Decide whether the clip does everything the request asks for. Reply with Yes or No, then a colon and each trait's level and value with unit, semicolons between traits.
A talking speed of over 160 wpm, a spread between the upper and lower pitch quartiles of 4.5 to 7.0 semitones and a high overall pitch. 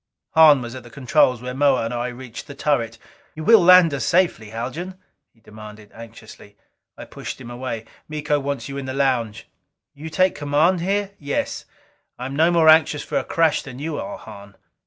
No: average, 195 wpm; average, 5.0 semitones; medium, 140 Hz